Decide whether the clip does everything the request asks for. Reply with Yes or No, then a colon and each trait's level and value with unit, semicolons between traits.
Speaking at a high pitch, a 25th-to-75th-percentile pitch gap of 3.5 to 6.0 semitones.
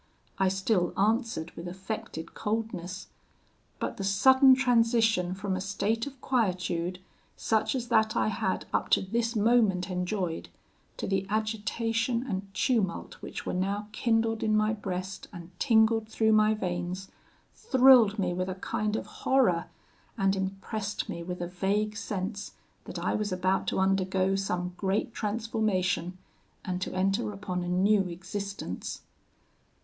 No: high, 200 Hz; average, 3.1 semitones